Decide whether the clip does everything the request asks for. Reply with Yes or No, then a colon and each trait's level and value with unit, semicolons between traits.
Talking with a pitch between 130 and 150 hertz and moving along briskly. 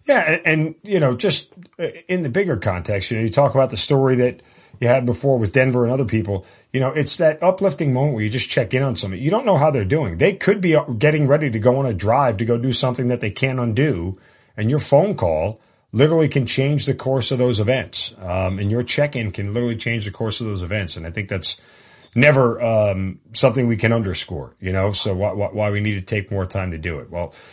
No: low, 120 Hz; fast, 255 wpm